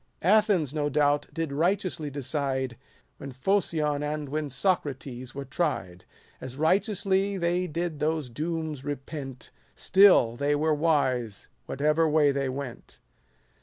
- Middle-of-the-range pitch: Yes, medium, 150 Hz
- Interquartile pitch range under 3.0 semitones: No, average, 3.4 semitones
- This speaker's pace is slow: Yes, slow, 125 wpm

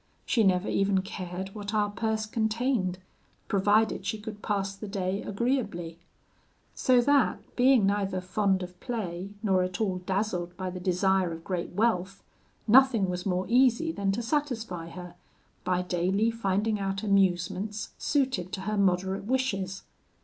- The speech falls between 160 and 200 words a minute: No, average, 150 wpm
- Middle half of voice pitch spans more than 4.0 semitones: No, average, 3.1 semitones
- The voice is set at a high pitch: Yes, high, 195 Hz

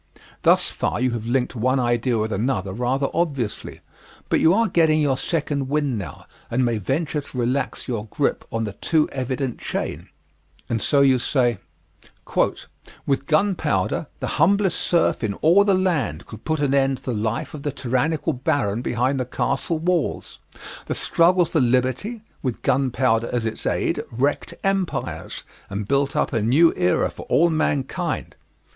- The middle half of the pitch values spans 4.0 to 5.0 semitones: Yes, average, 4.7 semitones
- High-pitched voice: No, low, 135 Hz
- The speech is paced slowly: No, average, 165 wpm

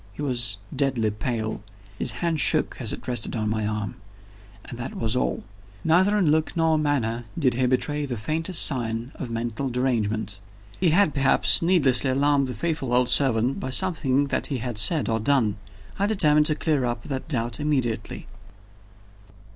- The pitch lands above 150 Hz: No, low, 130 Hz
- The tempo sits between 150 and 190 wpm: Yes, average, 170 wpm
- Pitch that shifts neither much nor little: Yes, average, 4.5 semitones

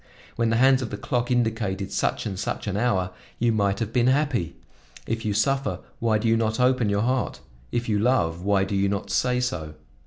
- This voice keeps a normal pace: No, fast, 215 wpm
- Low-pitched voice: Yes, low, 110 Hz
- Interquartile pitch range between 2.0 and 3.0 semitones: No, average, 3.7 semitones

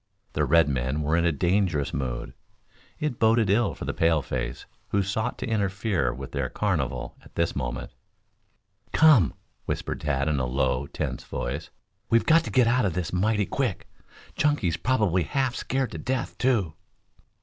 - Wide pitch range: Yes, wide, 8.4 semitones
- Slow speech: No, average, 165 wpm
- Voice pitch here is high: No, very low, 90 Hz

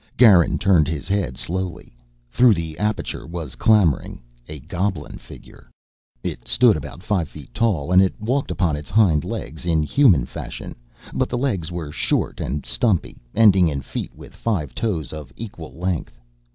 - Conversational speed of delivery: Yes, average, 165 wpm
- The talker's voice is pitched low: Yes, very low, 85 Hz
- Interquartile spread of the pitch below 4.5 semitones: No, wide, 5.4 semitones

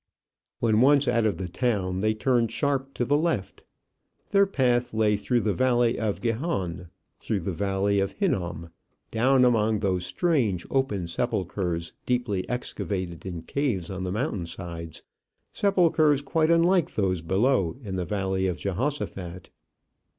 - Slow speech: No, average, 145 wpm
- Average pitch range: No, wide, 5.9 semitones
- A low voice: Yes, low, 110 Hz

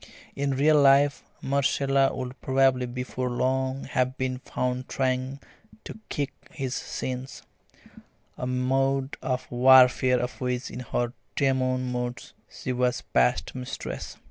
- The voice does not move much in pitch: Yes, narrow, 1.1 semitones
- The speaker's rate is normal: No, slow, 125 wpm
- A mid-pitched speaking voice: No, low, 130 Hz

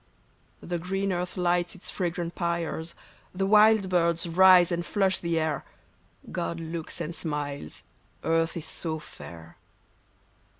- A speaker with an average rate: No, slow, 130 wpm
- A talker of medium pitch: Yes, medium, 170 Hz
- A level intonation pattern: Yes, narrow, 1.8 semitones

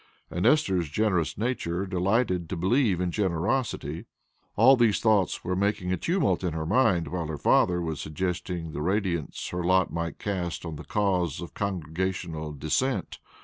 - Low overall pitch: Yes, very low, 90 Hz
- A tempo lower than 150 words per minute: No, average, 160 wpm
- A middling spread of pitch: Yes, average, 3.4 semitones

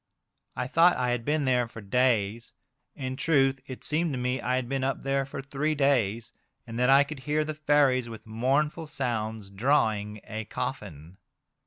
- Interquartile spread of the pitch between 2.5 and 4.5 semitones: Yes, average, 3.8 semitones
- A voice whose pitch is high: No, low, 130 Hz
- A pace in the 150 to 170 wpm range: No, average, 180 wpm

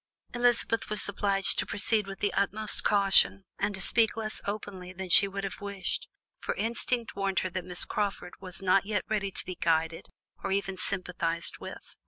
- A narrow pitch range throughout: Yes, narrow, 2.1 semitones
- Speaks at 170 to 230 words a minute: Yes, average, 185 wpm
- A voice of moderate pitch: No, high, 195 Hz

